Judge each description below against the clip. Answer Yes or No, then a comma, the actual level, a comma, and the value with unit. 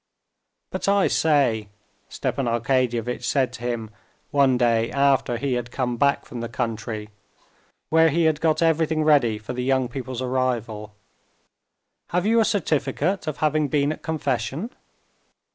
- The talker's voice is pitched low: Yes, low, 130 Hz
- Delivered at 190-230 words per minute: No, average, 145 wpm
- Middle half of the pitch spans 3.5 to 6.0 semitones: Yes, average, 4.4 semitones